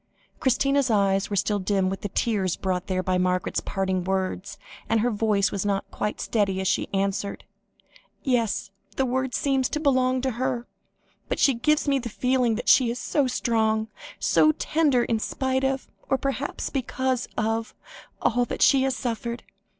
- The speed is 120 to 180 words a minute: Yes, average, 175 wpm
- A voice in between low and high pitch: No, high, 230 Hz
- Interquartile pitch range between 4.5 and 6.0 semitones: Yes, average, 4.8 semitones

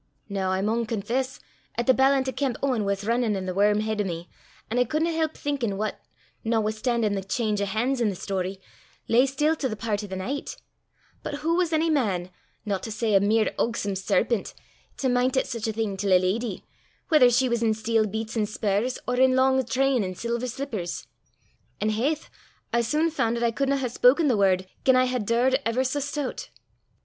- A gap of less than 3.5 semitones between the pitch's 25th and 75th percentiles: No, average, 4.1 semitones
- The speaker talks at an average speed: No, fast, 210 wpm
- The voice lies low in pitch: No, high, 230 Hz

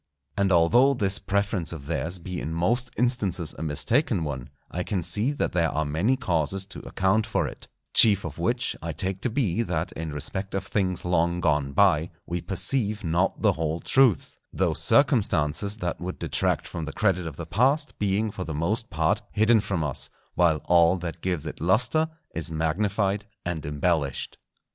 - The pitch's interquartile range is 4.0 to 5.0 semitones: Yes, average, 4.4 semitones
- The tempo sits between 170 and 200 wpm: Yes, average, 180 wpm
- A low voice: Yes, very low, 90 Hz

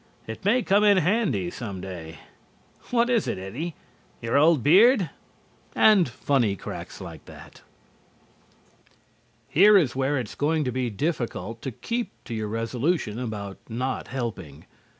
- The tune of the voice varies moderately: No, wide, 8.3 semitones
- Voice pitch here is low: Yes, low, 130 Hz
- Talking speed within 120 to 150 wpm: Yes, average, 145 wpm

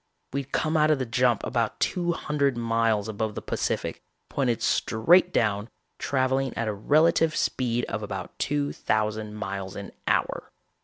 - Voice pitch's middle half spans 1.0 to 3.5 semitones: No, average, 4.8 semitones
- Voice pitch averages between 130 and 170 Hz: No, low, 120 Hz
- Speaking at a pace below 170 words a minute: Yes, average, 155 wpm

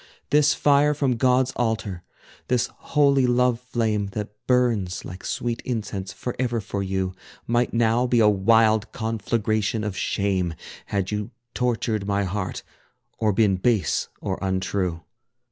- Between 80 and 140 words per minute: Yes, slow, 135 wpm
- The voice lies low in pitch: Yes, low, 110 Hz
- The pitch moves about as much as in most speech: Yes, average, 3.8 semitones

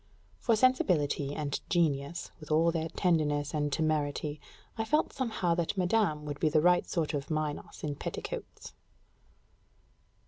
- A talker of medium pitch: Yes, medium, 155 Hz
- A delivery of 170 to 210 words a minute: No, average, 140 wpm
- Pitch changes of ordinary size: Yes, average, 3.2 semitones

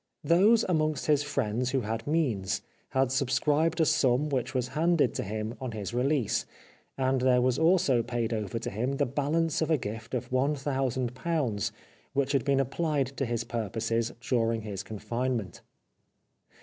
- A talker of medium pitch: No, low, 130 Hz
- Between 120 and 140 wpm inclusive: No, average, 170 wpm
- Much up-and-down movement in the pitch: No, average, 4.0 semitones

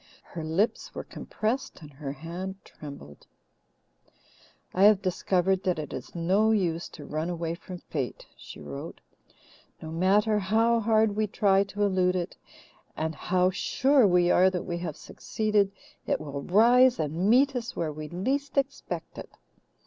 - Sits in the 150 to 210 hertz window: Yes, medium, 185 Hz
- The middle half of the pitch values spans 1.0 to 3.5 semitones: No, average, 4.7 semitones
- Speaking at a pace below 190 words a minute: Yes, average, 155 wpm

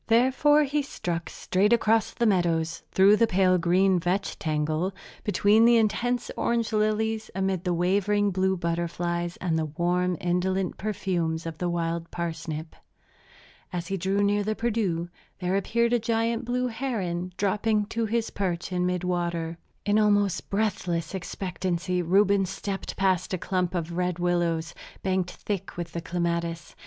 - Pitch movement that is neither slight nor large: Yes, average, 3.4 semitones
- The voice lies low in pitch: No, medium, 185 Hz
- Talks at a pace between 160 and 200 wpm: No, average, 150 wpm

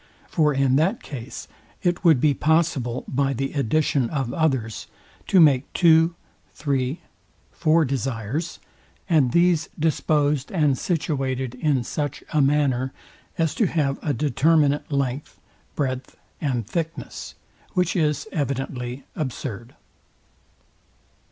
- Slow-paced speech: Yes, slow, 115 wpm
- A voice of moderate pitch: Yes, medium, 145 Hz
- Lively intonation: No, average, 3.5 semitones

